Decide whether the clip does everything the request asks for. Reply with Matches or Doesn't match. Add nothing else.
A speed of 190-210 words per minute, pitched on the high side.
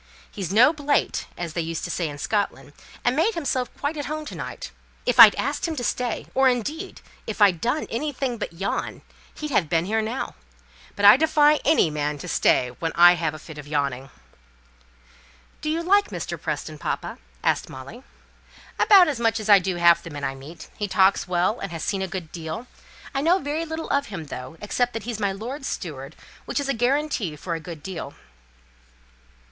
Matches